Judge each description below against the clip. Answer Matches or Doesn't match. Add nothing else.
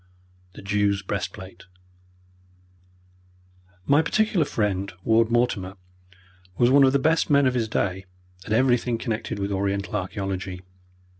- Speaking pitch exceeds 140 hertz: Doesn't match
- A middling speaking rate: Doesn't match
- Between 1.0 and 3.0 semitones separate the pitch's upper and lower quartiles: Doesn't match